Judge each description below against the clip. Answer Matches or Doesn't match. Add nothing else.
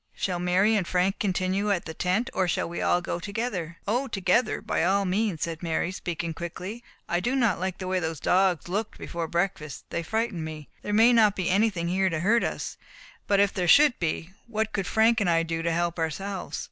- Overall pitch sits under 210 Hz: Matches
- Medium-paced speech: Doesn't match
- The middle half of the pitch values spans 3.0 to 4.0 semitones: Matches